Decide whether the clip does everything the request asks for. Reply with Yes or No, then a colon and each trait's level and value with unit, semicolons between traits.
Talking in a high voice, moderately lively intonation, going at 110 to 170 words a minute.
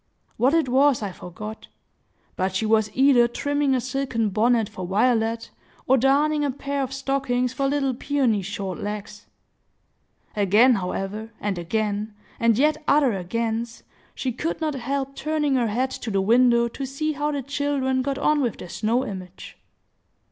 Yes: high, 245 Hz; average, 4.4 semitones; average, 160 wpm